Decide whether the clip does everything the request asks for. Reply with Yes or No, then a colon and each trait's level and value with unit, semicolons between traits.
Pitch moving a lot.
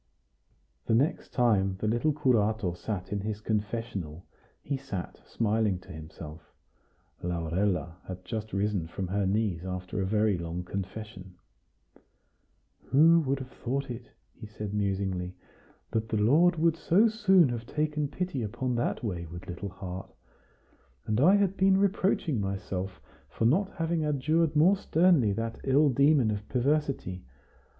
Yes: wide, 7.3 semitones